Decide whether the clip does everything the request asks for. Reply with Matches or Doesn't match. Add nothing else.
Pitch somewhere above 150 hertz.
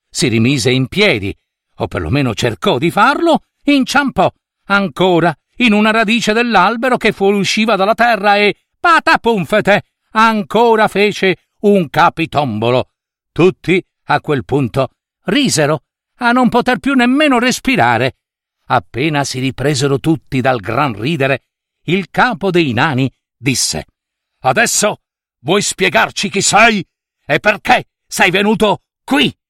Matches